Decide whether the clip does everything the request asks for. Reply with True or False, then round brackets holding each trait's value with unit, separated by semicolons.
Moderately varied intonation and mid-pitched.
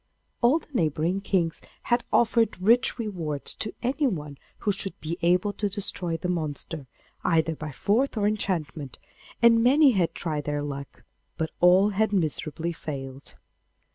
False (5.7 semitones; 180 Hz)